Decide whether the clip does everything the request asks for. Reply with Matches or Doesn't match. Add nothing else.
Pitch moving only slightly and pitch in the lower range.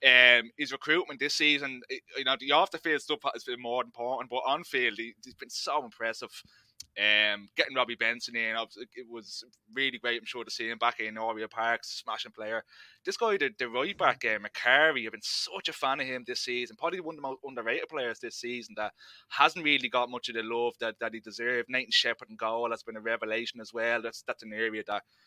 Matches